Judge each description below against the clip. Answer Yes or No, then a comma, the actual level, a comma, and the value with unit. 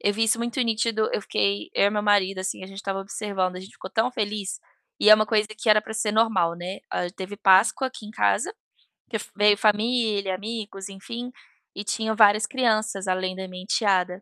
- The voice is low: No, high, 205 Hz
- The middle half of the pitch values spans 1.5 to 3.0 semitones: Yes, narrow, 2.5 semitones